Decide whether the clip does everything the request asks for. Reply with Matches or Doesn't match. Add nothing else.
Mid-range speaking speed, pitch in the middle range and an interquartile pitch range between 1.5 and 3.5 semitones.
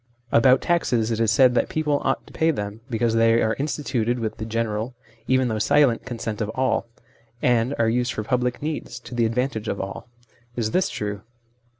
Doesn't match